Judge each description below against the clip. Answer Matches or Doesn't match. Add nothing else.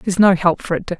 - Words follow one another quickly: Matches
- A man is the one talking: Doesn't match